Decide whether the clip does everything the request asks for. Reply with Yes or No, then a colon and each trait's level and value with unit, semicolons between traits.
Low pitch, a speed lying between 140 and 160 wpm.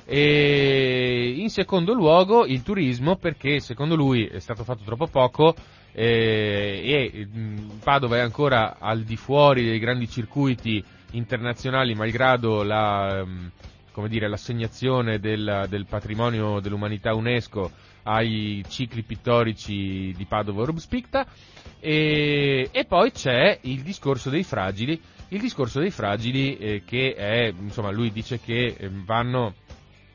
No: low, 115 Hz; average, 120 wpm